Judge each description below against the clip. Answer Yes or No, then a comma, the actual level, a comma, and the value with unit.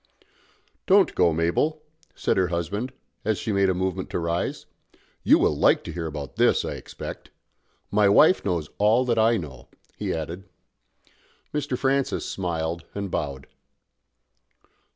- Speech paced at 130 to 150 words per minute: Yes, average, 145 wpm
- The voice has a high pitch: No, very low, 95 Hz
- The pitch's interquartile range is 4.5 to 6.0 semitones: Yes, average, 4.9 semitones